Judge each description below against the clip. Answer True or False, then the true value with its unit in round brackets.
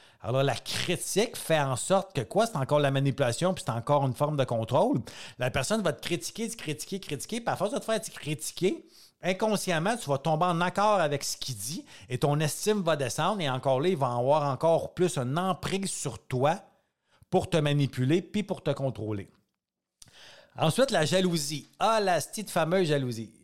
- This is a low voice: False (155 Hz)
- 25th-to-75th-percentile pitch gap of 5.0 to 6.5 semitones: True (5.4 semitones)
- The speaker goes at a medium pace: True (200 wpm)